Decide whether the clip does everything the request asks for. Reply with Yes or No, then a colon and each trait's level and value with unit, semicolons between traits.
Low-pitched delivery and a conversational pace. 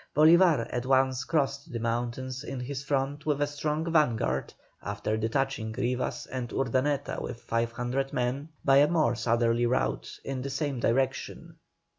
Yes: low, 130 Hz; average, 150 wpm